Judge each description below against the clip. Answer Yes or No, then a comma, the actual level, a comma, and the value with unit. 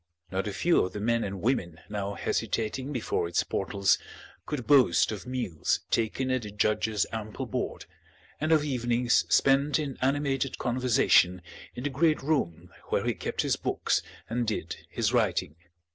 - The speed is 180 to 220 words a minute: No, average, 160 wpm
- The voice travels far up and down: No, average, 4.9 semitones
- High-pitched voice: No, low, 120 Hz